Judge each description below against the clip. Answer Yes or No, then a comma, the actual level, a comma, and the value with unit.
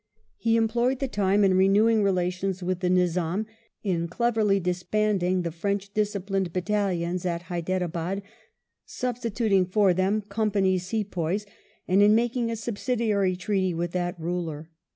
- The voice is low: No, high, 195 Hz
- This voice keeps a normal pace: No, slow, 130 wpm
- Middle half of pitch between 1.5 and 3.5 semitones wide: Yes, average, 3.0 semitones